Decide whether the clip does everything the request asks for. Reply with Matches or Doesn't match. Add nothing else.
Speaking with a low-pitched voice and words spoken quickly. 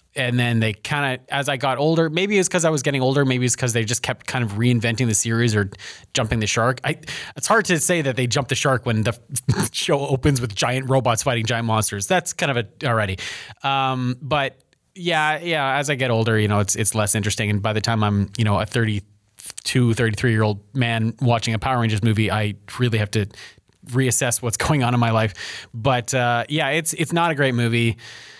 Matches